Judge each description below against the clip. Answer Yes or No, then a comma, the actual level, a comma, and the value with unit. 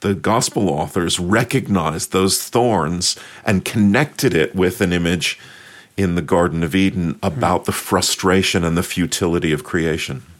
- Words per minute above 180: No, average, 145 wpm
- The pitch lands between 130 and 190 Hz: No, very low, 90 Hz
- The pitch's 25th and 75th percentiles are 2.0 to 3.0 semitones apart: Yes, narrow, 2.6 semitones